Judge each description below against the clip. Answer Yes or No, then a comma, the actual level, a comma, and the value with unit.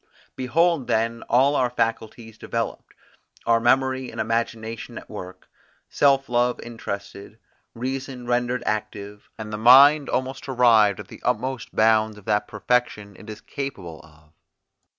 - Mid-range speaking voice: No, low, 115 Hz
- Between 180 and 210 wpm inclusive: No, slow, 135 wpm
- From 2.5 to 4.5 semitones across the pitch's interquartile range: Yes, average, 3.2 semitones